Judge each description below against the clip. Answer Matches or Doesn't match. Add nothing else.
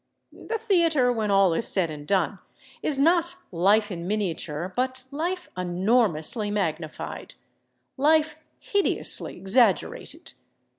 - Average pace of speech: Doesn't match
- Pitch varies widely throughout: Matches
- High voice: Matches